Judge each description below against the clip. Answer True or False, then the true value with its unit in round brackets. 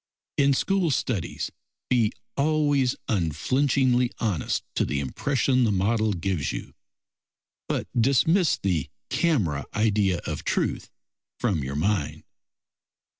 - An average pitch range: False (7.0 semitones)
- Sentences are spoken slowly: True (110 wpm)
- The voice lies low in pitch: True (115 Hz)